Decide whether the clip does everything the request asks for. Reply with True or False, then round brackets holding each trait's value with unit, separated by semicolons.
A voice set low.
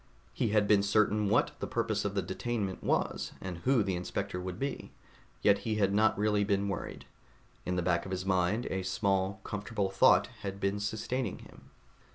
True (100 Hz)